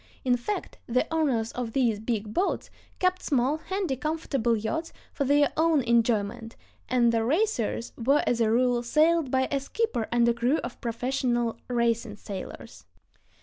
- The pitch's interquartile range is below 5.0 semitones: Yes, average, 4.0 semitones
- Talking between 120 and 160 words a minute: Yes, average, 150 wpm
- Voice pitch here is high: Yes, high, 245 Hz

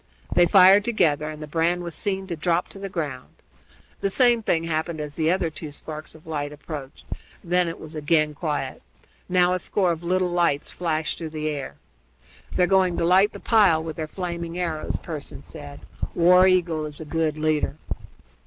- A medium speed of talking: Yes, average, 190 wpm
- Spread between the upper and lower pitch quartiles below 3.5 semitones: Yes, average, 2.7 semitones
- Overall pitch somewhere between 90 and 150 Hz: No, medium, 165 Hz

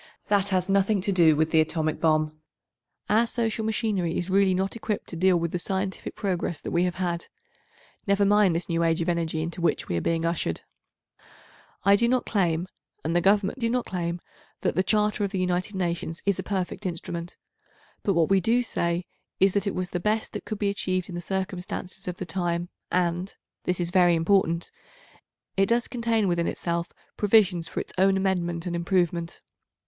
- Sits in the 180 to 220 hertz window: Yes, medium, 185 Hz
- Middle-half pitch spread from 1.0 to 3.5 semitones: Yes, average, 2.7 semitones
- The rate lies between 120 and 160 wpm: No, average, 190 wpm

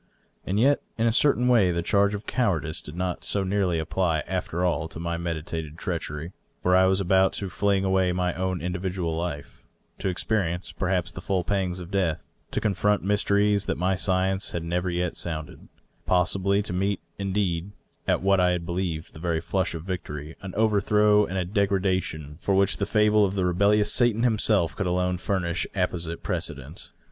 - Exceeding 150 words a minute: Yes, average, 190 wpm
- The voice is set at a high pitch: No, very low, 95 Hz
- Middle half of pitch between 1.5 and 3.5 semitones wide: Yes, narrow, 2.6 semitones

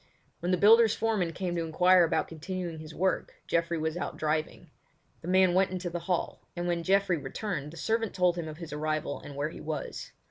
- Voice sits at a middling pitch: Yes, medium, 175 Hz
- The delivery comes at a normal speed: No, fast, 210 wpm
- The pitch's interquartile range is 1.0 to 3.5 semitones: Yes, average, 2.8 semitones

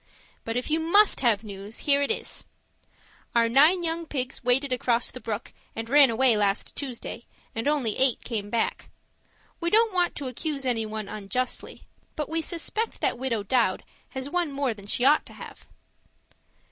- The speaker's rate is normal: Yes, average, 170 wpm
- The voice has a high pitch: Yes, very high, 255 Hz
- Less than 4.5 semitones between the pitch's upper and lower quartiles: No, average, 4.8 semitones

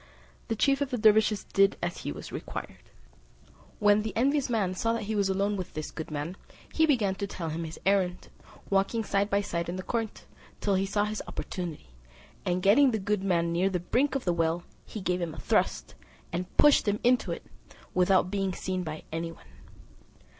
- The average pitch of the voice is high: Yes, high, 195 Hz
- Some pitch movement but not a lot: Yes, average, 3.4 semitones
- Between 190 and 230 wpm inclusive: Yes, fast, 205 wpm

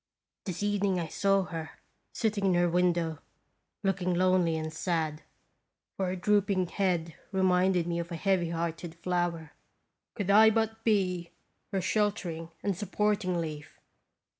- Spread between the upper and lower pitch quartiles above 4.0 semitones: No, average, 2.7 semitones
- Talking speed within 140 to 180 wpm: Yes, average, 145 wpm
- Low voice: No, medium, 180 Hz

